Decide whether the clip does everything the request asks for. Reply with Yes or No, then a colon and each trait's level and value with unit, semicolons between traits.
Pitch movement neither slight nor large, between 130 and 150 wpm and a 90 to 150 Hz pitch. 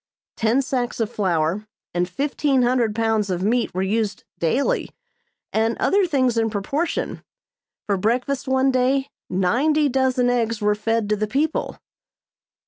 No: average, 4.1 semitones; average, 140 wpm; high, 230 Hz